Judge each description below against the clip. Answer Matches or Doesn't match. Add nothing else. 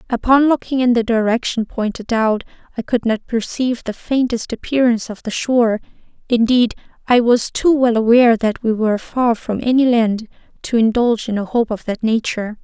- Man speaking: Doesn't match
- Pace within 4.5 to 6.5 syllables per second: Matches